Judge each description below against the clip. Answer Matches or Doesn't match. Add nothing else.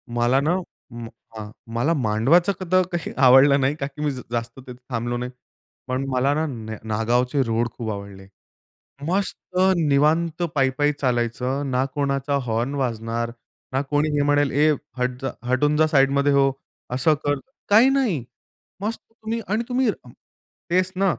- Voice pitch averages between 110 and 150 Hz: Matches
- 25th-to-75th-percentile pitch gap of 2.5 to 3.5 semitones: Doesn't match